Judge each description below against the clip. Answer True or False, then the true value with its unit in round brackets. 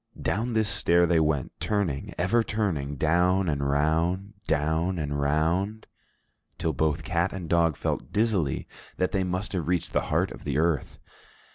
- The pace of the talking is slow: False (160 wpm)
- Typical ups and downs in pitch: True (3.6 semitones)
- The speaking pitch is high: False (85 Hz)